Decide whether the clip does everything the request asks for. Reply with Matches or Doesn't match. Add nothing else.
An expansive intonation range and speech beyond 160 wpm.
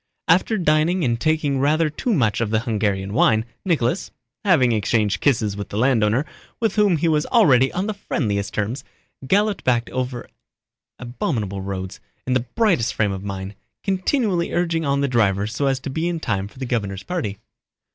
Matches